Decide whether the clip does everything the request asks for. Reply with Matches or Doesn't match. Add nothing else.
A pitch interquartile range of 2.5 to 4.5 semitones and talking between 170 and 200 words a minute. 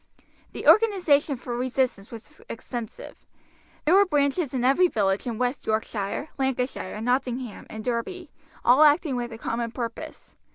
Doesn't match